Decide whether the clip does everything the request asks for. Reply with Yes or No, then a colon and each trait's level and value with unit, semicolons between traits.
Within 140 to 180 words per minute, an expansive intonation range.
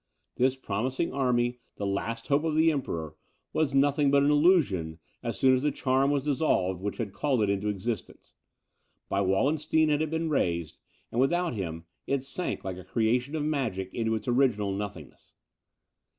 Yes: average, 175 wpm; wide, 6.4 semitones